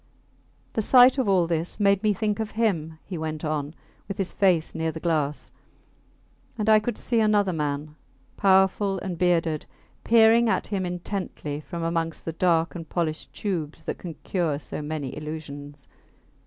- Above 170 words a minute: No, average, 165 wpm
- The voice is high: No, medium, 175 Hz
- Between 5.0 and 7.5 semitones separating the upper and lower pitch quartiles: No, average, 4.4 semitones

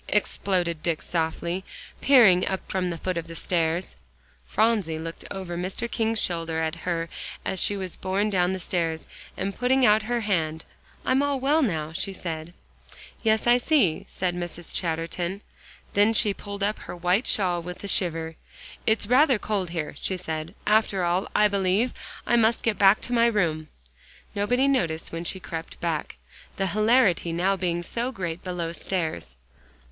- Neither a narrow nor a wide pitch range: Yes, average, 4.1 semitones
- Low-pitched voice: No, medium, 185 Hz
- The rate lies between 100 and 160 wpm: No, average, 170 wpm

